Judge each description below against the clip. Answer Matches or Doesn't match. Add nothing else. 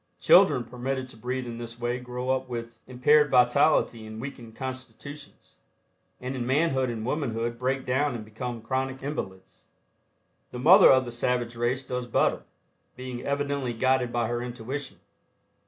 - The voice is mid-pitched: Doesn't match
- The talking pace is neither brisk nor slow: Matches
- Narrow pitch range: Matches